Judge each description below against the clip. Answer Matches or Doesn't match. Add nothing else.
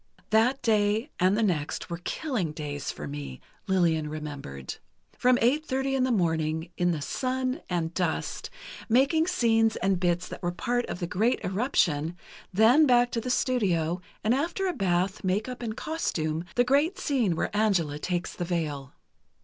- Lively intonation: Matches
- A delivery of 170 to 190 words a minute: Matches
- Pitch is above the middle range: Matches